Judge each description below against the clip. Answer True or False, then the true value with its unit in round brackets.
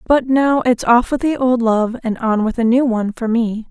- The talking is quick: True (260 wpm)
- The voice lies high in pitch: True (240 Hz)